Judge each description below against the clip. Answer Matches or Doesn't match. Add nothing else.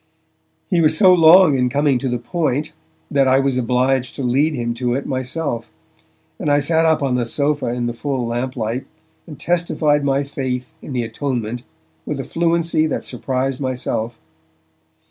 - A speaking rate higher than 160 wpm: Matches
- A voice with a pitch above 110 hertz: Matches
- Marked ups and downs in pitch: Doesn't match